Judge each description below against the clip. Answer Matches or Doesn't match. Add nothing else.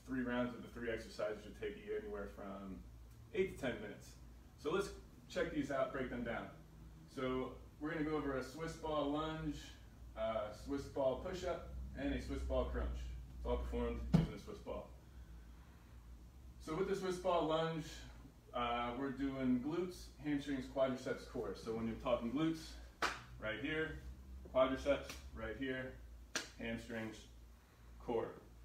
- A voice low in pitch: Matches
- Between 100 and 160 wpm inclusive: Matches